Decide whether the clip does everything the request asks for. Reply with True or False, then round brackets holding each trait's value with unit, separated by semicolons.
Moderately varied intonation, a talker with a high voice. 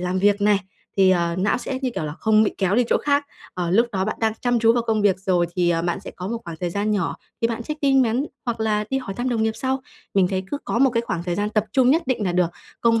True (4.4 semitones; 210 Hz)